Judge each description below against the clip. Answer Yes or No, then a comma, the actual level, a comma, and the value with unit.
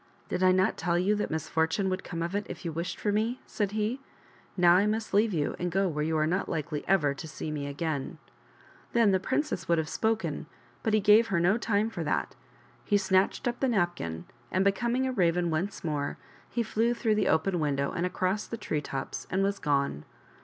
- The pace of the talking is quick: Yes, fast, 225 wpm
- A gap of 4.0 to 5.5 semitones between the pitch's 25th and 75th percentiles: Yes, average, 4.7 semitones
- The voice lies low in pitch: No, medium, 185 Hz